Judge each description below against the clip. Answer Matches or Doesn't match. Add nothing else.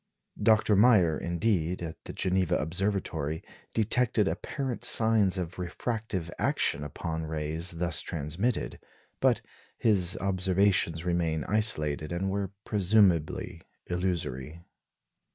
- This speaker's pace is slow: Matches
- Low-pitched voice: Matches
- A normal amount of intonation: Matches